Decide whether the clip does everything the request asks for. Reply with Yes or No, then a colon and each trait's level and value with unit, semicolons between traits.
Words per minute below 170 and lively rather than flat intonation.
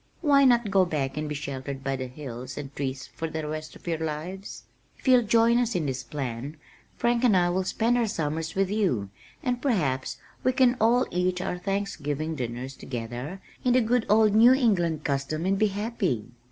No: average, 195 wpm; wide, 8.1 semitones